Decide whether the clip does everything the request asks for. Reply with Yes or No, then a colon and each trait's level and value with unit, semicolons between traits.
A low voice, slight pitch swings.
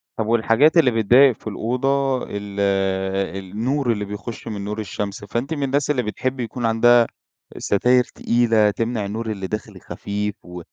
No: low, 115 Hz; average, 3.3 semitones